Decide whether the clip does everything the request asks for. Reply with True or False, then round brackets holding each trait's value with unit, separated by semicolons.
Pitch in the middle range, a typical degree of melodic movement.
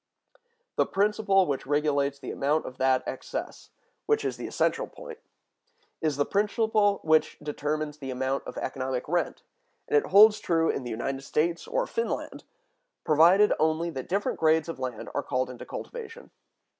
False (160 Hz; 7.0 semitones)